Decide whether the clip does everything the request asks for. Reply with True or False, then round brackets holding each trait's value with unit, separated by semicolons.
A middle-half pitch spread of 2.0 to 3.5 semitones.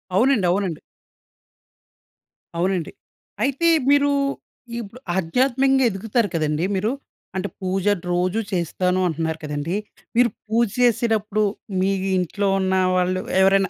False (4.4 semitones)